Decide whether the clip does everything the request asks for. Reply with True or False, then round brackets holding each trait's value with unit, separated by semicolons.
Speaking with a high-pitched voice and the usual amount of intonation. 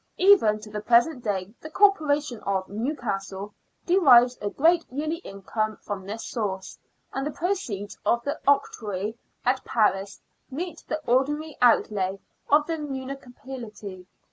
False (240 Hz; 6.3 semitones)